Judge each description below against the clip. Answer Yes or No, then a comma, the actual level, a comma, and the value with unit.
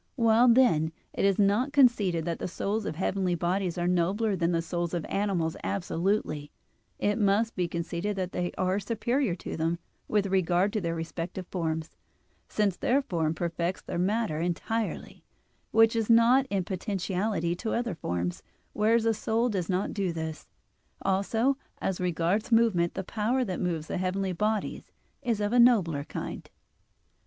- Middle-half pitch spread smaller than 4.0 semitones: No, average, 4.3 semitones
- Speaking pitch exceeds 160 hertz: Yes, high, 190 Hz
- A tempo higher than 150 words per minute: Yes, average, 165 wpm